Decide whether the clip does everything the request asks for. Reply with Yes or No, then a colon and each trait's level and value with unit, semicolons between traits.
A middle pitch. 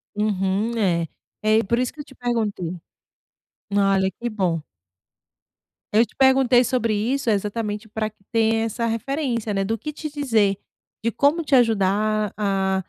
No: high, 220 Hz